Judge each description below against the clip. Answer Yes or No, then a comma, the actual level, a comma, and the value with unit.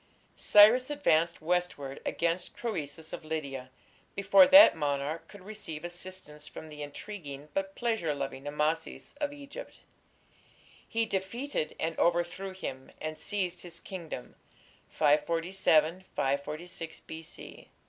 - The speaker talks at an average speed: No, slow, 115 wpm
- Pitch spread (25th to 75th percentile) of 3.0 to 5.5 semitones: Yes, average, 4.3 semitones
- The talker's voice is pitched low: No, medium, 170 Hz